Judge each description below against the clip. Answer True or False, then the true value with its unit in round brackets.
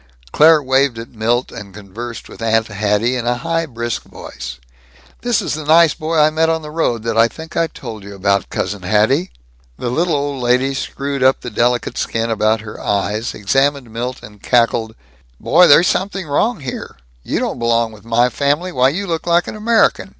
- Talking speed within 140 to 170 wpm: False (195 wpm)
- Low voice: True (125 Hz)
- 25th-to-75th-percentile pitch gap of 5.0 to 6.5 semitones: True (5.5 semitones)